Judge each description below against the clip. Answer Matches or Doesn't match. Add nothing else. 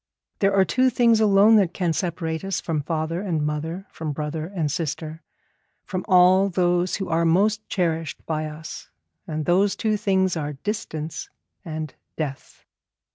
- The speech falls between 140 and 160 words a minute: Matches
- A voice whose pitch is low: Doesn't match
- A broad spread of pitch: Doesn't match